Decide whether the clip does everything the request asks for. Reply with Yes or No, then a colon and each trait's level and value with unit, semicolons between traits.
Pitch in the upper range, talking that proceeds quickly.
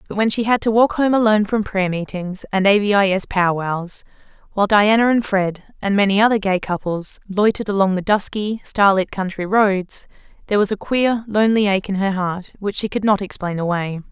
Yes: high, 200 Hz; fast, 210 wpm